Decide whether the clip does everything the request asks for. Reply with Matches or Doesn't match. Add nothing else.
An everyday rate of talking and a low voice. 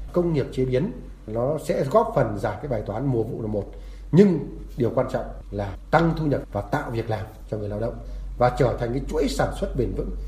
Matches